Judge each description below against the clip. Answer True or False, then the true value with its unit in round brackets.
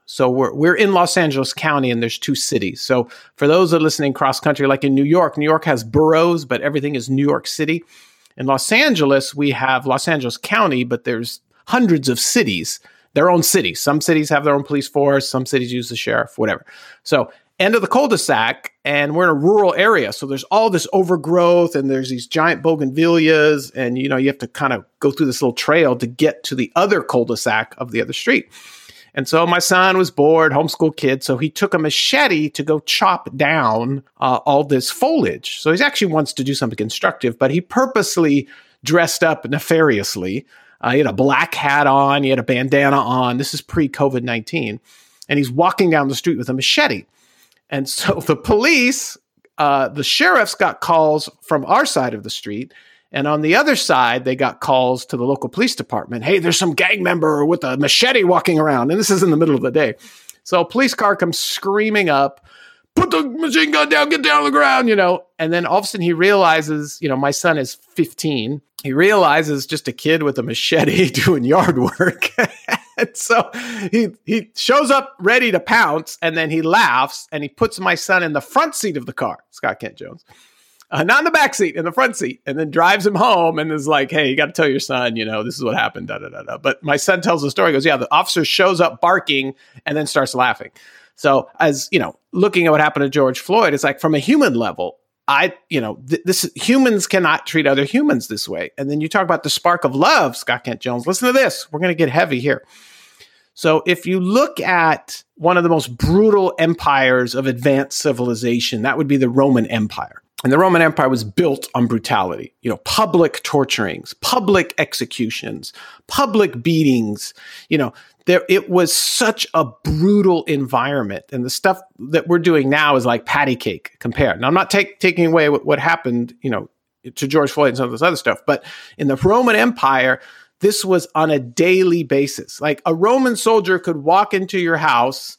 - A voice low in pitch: False (155 Hz)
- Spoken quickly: True (215 wpm)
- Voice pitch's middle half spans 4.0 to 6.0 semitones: True (5.1 semitones)